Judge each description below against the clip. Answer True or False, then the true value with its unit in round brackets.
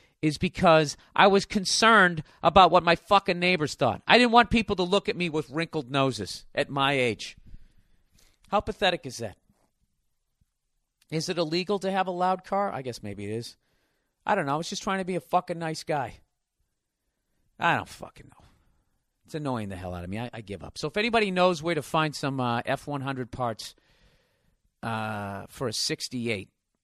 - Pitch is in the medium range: True (155 Hz)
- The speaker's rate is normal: True (190 wpm)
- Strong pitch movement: True (7.6 semitones)